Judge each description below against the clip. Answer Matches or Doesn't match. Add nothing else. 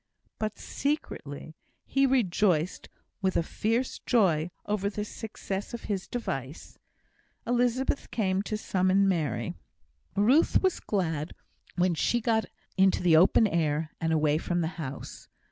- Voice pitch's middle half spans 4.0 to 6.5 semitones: Matches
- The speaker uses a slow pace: Matches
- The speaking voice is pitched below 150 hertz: Doesn't match